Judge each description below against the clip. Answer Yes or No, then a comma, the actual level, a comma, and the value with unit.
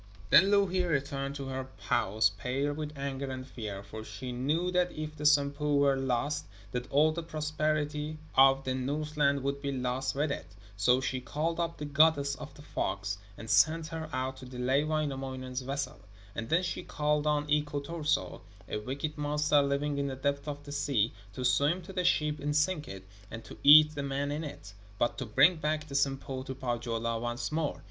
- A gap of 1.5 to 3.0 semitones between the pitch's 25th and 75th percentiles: Yes, average, 2.7 semitones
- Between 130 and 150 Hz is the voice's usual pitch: Yes, medium, 140 Hz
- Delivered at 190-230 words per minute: Yes, average, 195 wpm